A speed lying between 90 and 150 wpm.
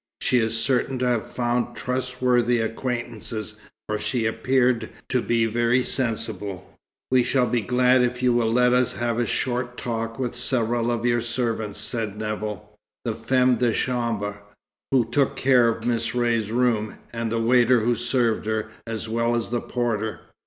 No: average, 165 wpm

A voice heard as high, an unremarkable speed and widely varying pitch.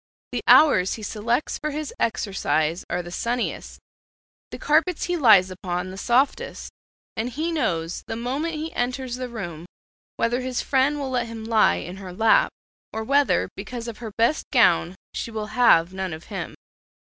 Yes: high, 230 Hz; average, 170 wpm; wide, 5.8 semitones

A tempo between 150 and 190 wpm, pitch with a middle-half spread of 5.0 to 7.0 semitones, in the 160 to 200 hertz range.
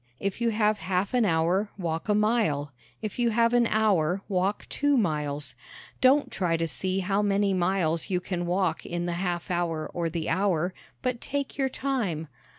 No: average, 180 wpm; average, 4.2 semitones; high, 190 Hz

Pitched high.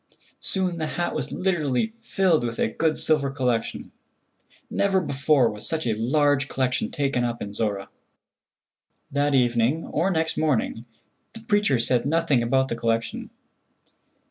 No: medium, 140 Hz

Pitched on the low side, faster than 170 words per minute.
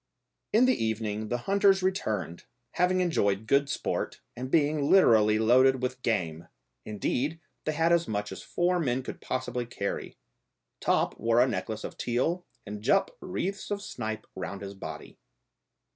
No: low, 125 Hz; average, 155 wpm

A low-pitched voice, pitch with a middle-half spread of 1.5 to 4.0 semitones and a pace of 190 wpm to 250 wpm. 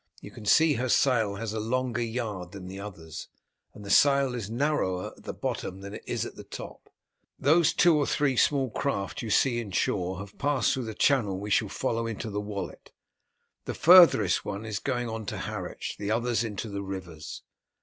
No: low, 110 Hz; average, 4.4 semitones; average, 200 wpm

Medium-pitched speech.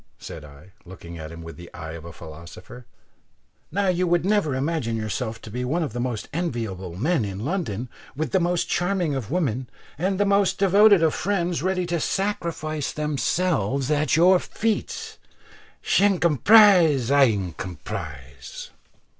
Yes: medium, 145 Hz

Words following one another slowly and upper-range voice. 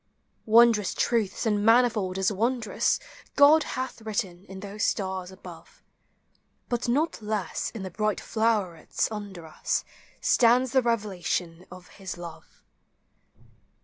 Yes: slow, 120 wpm; high, 210 Hz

